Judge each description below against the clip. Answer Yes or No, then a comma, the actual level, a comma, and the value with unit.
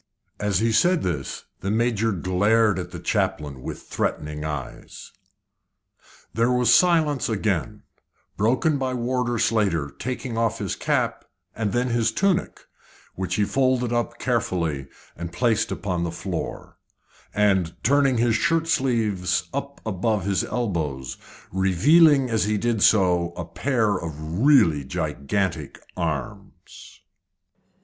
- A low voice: Yes, low, 105 Hz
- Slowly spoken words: Yes, slow, 125 wpm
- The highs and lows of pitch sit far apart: Yes, wide, 5.9 semitones